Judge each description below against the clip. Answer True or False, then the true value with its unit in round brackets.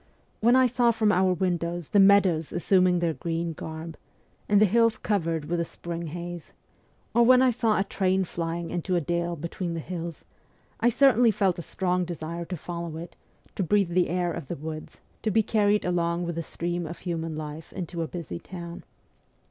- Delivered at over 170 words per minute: True (195 wpm)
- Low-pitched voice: False (175 Hz)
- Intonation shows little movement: False (3.0 semitones)